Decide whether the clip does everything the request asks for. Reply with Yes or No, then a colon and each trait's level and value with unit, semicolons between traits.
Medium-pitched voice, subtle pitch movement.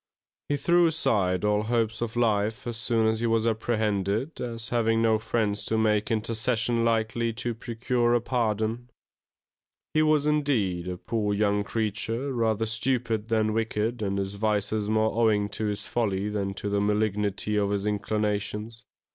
No: low, 110 Hz; narrow, 2.0 semitones